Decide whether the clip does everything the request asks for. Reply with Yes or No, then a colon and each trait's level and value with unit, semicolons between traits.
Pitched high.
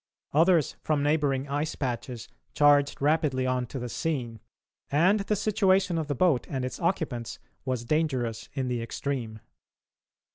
No: medium, 140 Hz